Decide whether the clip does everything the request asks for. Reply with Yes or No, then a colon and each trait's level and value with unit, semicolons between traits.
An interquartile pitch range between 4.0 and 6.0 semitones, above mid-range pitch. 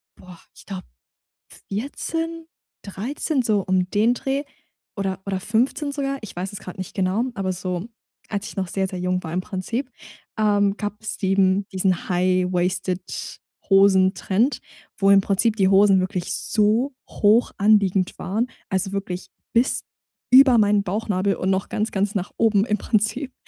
No: average, 2.8 semitones; high, 200 Hz